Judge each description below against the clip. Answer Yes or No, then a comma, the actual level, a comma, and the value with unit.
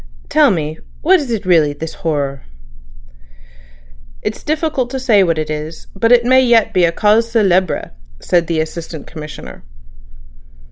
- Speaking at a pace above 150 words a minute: No, average, 145 wpm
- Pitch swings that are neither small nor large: No, wide, 7.0 semitones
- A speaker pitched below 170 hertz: No, medium, 180 Hz